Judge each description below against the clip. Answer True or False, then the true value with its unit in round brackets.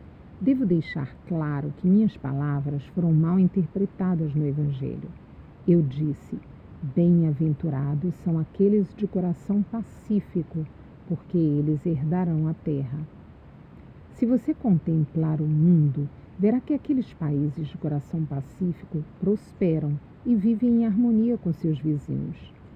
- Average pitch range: True (4.6 semitones)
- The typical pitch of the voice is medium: True (165 Hz)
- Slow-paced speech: True (115 wpm)